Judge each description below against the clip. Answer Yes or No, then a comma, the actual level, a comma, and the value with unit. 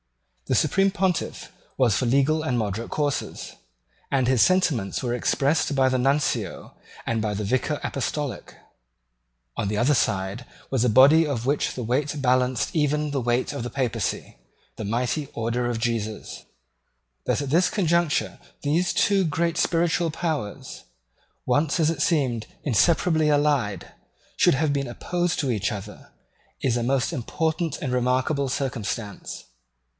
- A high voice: No, low, 135 Hz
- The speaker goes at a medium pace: Yes, average, 150 wpm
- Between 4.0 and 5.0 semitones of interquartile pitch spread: Yes, average, 4.4 semitones